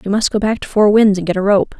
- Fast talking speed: Yes, fast, 370 wpm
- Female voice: Yes, female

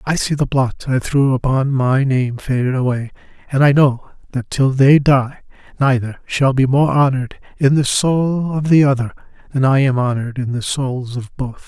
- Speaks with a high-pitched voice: No, low, 135 Hz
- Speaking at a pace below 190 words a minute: No, average, 195 wpm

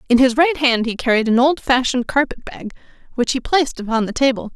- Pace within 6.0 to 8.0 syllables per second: Yes, 6.1 syllables/s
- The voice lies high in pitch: Yes, very high, 255 Hz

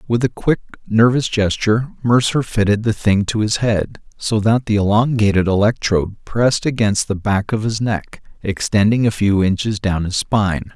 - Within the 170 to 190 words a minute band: Yes, average, 175 wpm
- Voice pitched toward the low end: Yes, low, 105 Hz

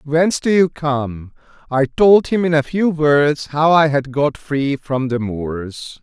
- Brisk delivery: No, average, 190 wpm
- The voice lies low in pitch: No, medium, 145 Hz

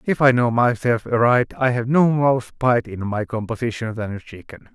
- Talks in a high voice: No, low, 120 Hz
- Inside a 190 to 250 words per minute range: Yes, average, 200 wpm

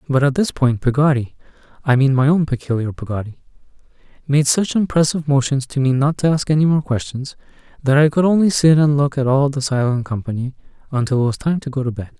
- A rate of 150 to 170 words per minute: No, average, 200 wpm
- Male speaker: Yes, male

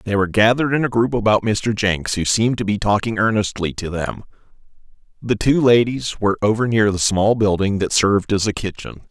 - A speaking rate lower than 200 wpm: No, fast, 205 wpm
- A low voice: Yes, low, 105 Hz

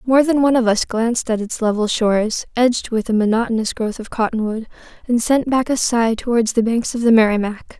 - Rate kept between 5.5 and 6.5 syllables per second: Yes, 5.7 syllables/s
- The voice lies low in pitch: No, high, 230 Hz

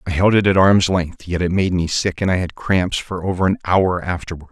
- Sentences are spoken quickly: Yes, fast, 265 wpm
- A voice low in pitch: Yes, very low, 95 Hz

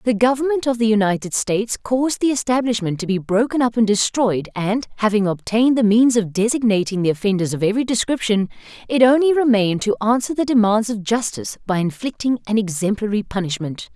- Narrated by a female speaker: Yes, female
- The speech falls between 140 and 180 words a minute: Yes, average, 175 wpm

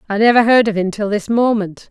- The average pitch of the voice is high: Yes, high, 215 Hz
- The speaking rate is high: Yes, fast, 250 wpm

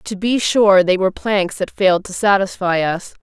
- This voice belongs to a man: No, female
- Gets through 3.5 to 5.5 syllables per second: Yes, 4.9 syllables/s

